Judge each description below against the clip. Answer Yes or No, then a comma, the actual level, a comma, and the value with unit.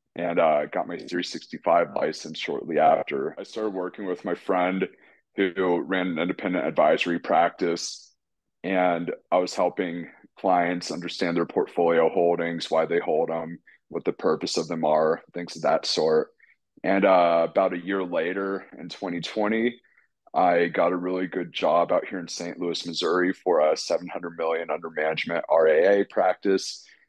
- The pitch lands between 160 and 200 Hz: No, very low, 90 Hz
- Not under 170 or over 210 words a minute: No, average, 160 wpm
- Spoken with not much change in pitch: Yes, narrow, 2.2 semitones